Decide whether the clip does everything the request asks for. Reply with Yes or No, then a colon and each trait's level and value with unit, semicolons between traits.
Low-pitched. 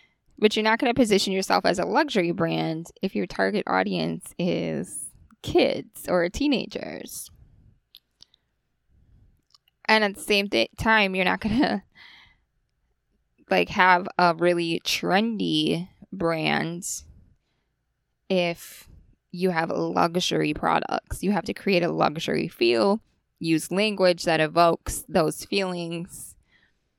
No: medium, 180 Hz